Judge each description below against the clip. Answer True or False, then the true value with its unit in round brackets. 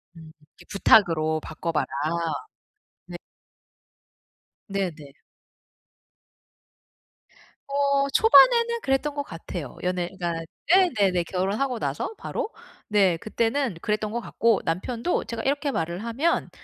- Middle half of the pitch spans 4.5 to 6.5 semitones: False (8.2 semitones)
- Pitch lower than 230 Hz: True (210 Hz)